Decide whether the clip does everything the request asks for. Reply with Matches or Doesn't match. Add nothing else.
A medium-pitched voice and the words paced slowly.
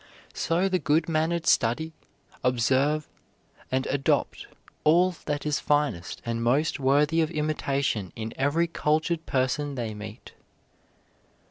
Matches